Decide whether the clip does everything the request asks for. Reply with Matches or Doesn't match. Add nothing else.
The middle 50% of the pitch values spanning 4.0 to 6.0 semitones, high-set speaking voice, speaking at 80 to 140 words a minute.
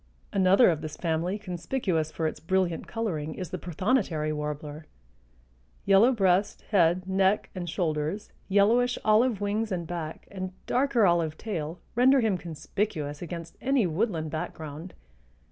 Doesn't match